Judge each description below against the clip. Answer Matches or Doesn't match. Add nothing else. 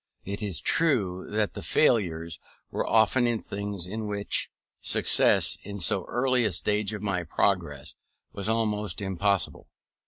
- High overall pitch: Doesn't match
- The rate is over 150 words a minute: Doesn't match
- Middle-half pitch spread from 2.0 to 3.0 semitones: Matches